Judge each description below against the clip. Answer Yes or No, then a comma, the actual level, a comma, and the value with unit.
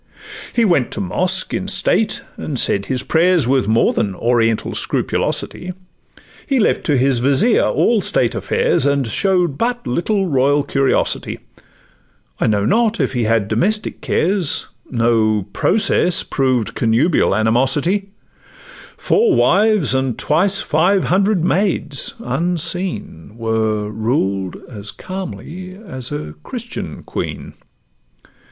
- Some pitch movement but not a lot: No, wide, 8.6 semitones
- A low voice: No, medium, 145 Hz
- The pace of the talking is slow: Yes, slow, 120 wpm